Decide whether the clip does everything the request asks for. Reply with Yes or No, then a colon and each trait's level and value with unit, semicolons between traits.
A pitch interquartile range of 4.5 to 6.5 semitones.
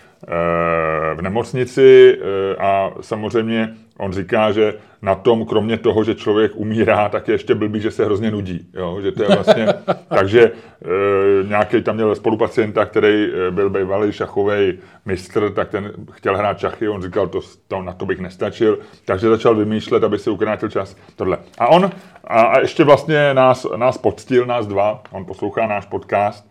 No: average, 3.1 semitones